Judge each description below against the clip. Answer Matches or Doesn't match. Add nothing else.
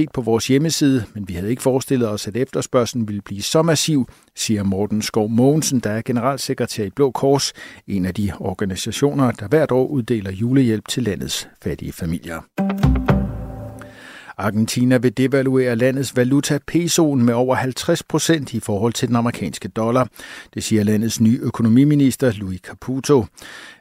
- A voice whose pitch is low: Matches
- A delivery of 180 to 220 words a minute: Doesn't match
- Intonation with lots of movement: Doesn't match